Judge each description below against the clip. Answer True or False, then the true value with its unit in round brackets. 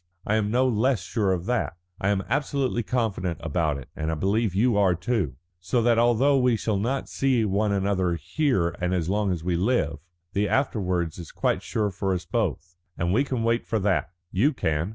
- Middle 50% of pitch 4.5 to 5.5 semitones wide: True (5.1 semitones)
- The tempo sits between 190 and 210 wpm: True (205 wpm)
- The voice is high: False (100 Hz)